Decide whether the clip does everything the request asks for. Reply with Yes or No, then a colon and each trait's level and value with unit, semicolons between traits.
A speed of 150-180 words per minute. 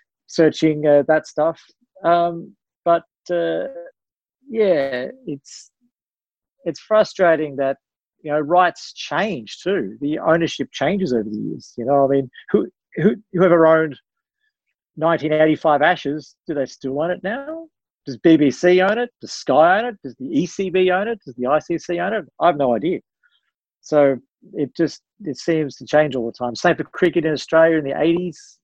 Yes: average, 170 wpm